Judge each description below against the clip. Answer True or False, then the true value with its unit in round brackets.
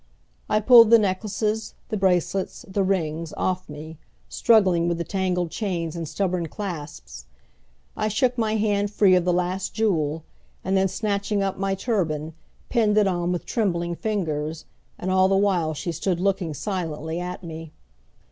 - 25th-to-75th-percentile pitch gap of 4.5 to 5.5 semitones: False (3.4 semitones)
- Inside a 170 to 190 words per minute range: False (160 wpm)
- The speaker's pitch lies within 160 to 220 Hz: True (185 Hz)